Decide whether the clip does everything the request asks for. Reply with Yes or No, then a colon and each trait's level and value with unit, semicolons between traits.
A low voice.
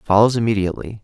Yes: low, 105 Hz